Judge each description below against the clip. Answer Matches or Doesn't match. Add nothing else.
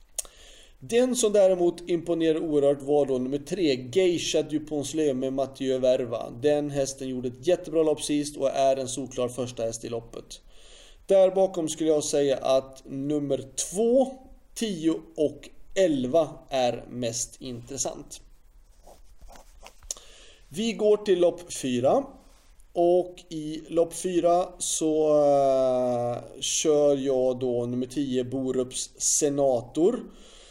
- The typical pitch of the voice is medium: Matches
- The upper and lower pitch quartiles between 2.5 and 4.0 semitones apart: Doesn't match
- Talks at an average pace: Doesn't match